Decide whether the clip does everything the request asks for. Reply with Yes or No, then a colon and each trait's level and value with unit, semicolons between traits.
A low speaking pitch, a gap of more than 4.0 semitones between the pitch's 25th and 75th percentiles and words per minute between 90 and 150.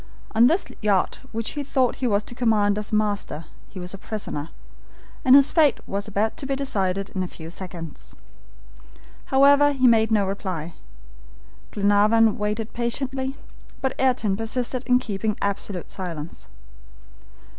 No: high, 215 Hz; average, 4.4 semitones; average, 145 wpm